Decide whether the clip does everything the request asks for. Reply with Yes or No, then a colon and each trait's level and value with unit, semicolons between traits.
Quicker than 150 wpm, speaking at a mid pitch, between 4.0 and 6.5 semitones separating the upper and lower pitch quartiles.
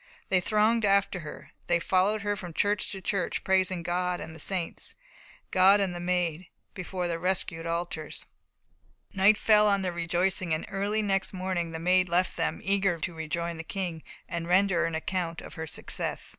No: average, 180 wpm; medium, 180 Hz; narrow, 2.5 semitones